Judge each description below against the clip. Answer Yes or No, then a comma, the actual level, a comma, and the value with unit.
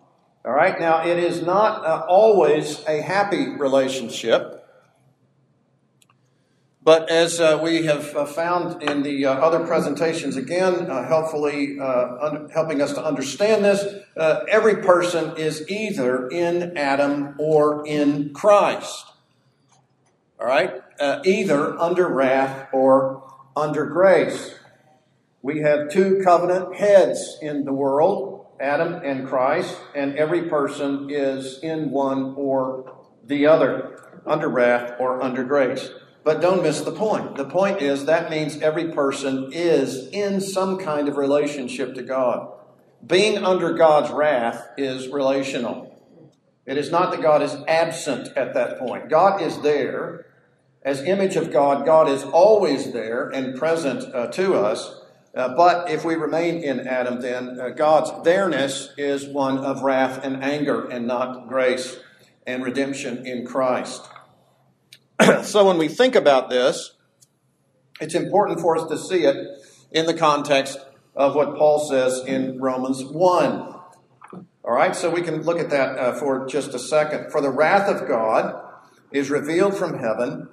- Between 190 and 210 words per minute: No, average, 145 wpm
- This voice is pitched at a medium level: Yes, medium, 150 Hz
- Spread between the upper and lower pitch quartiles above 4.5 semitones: No, average, 3.7 semitones